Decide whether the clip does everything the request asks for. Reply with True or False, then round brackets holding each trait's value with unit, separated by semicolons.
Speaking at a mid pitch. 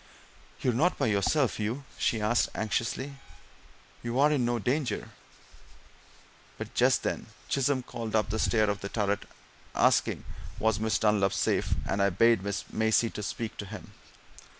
False (110 Hz)